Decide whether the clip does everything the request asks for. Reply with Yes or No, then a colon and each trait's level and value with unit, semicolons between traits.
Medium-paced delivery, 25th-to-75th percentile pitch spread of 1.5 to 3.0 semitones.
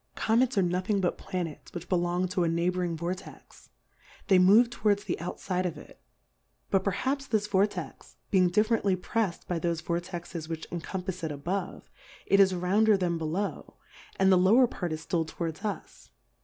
Yes: average, 180 wpm; average, 2.7 semitones